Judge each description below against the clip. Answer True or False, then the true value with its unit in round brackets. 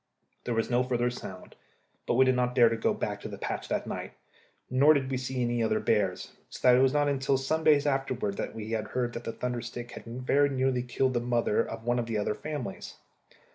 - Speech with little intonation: True (2.2 semitones)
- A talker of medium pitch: False (125 Hz)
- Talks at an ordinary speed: False (245 wpm)